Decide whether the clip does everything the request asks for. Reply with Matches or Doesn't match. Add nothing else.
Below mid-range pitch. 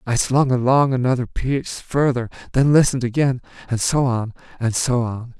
Matches